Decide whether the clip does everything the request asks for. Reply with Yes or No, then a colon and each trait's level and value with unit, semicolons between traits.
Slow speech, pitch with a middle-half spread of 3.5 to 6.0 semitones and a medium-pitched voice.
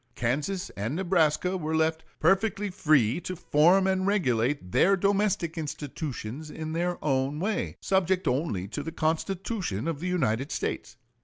No: average, 145 wpm; average, 4.7 semitones; medium, 160 Hz